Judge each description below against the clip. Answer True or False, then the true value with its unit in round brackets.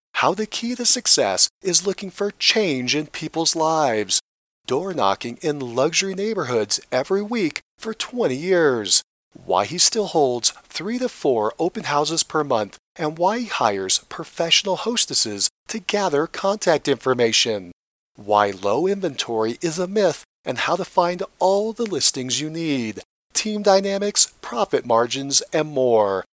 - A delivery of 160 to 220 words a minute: False (145 wpm)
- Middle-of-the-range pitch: True (165 Hz)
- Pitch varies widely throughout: True (7.6 semitones)